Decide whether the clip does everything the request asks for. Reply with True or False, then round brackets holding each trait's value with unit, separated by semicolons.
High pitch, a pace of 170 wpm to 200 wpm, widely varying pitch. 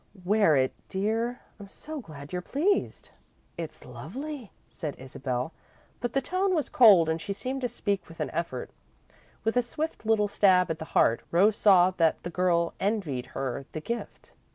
True (195 Hz; 175 wpm; 6.7 semitones)